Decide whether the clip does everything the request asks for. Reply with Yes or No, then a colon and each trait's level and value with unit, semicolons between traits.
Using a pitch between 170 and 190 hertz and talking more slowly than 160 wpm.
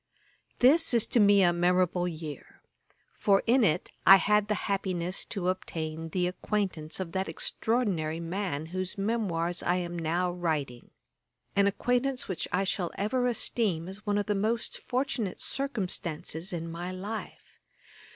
Yes: medium, 185 Hz; average, 150 wpm